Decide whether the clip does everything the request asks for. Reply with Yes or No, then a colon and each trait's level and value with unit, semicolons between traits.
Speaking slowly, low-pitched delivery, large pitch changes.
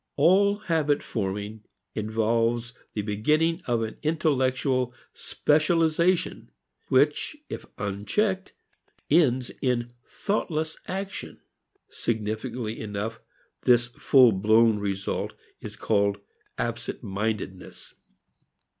Yes: slow, 80 wpm; low, 120 Hz; wide, 6.3 semitones